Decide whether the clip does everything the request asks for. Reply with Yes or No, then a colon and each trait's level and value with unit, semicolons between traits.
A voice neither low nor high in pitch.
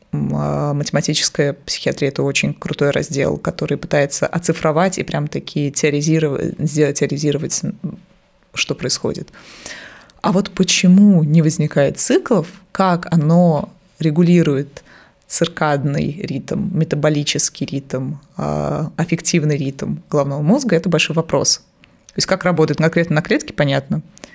Yes: medium, 155 Hz